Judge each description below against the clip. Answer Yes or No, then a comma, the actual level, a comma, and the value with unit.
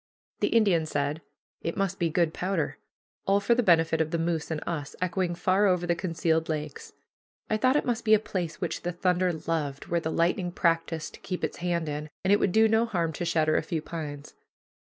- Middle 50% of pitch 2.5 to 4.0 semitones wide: Yes, average, 2.8 semitones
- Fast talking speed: Yes, fast, 220 wpm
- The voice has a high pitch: No, medium, 170 Hz